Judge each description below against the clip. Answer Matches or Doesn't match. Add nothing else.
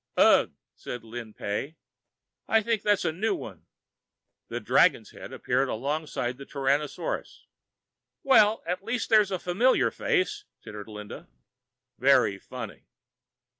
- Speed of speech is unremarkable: Doesn't match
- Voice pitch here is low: Doesn't match